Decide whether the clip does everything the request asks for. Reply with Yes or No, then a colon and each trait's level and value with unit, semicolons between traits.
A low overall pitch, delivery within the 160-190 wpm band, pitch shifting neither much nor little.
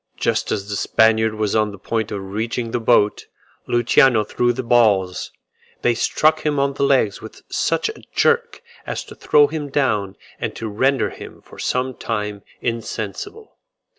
Yes: low, 115 Hz; average, 165 wpm; average, 4.2 semitones